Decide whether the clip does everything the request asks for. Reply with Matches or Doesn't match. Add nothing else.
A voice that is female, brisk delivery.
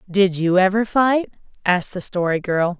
Doesn't match